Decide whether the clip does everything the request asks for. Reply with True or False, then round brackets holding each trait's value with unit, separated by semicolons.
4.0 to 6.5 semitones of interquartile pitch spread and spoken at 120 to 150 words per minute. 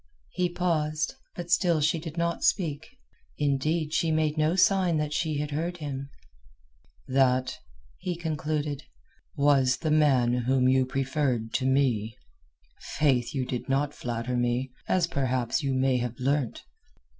False (3.5 semitones; 145 wpm)